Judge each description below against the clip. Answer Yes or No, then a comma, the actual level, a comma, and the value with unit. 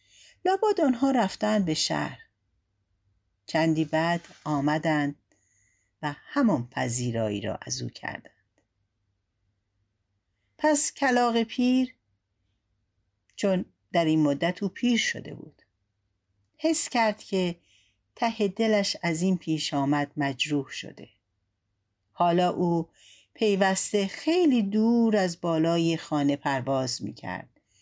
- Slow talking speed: Yes, slow, 100 wpm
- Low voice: No, medium, 155 Hz